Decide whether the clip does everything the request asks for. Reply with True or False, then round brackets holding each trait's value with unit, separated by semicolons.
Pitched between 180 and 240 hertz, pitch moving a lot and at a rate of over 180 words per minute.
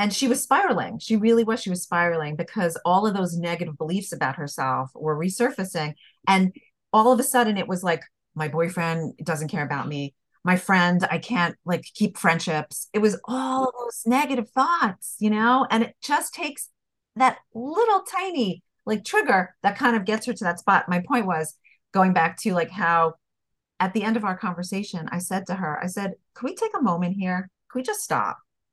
True (190 Hz; 6.0 semitones; 205 wpm)